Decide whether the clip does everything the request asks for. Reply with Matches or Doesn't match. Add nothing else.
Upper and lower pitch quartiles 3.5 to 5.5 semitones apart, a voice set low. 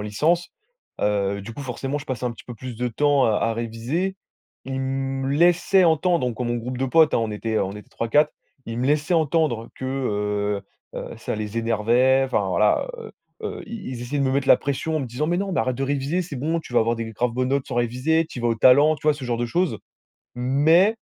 Matches